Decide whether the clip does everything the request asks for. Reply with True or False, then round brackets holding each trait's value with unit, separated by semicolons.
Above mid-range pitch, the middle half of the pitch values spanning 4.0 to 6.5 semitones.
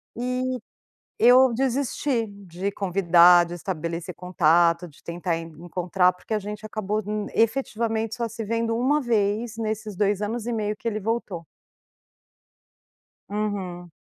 True (210 Hz; 4.3 semitones)